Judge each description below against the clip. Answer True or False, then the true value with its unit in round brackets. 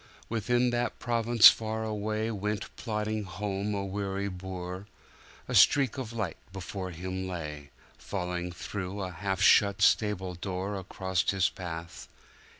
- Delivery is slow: True (125 wpm)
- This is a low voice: True (100 Hz)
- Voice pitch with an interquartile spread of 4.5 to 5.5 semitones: False (2.7 semitones)